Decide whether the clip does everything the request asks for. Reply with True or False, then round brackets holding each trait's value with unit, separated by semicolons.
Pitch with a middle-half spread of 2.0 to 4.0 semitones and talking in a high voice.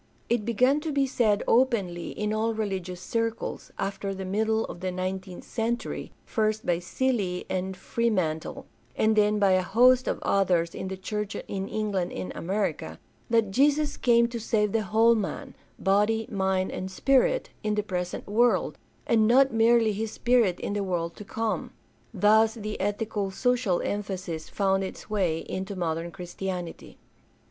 True (3.3 semitones; 210 Hz)